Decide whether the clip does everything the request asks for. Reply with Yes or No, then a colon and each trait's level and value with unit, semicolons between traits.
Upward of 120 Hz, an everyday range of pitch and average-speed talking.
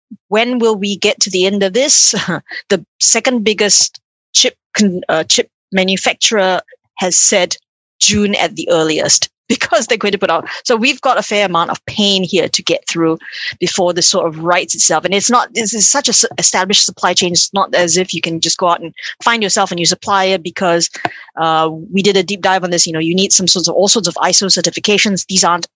No: high, 190 Hz; average, 3.1 semitones; fast, 220 wpm